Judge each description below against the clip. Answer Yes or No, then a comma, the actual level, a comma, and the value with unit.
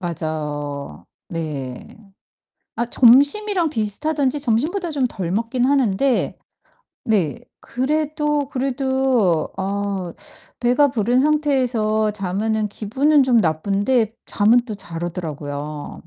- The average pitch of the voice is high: Yes, high, 225 Hz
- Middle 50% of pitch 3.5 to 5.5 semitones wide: No, wide, 6.8 semitones